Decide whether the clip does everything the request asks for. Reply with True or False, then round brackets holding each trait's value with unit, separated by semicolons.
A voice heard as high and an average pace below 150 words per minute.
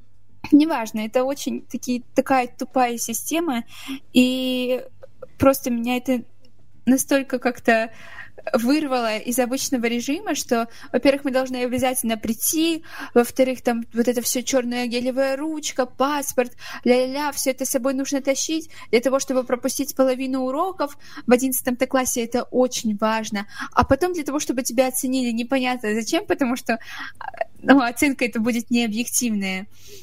True (260 Hz; 135 wpm)